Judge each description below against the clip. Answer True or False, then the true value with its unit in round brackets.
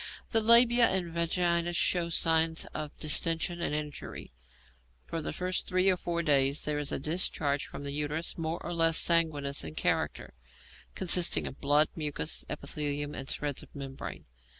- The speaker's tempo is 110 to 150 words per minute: False (160 wpm)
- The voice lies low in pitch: False (160 Hz)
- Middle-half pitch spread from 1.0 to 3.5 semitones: True (2.9 semitones)